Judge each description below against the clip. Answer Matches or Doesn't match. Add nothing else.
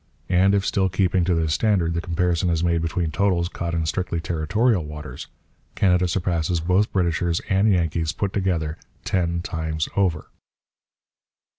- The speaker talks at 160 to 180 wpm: Doesn't match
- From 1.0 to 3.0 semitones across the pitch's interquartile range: Matches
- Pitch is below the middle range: Matches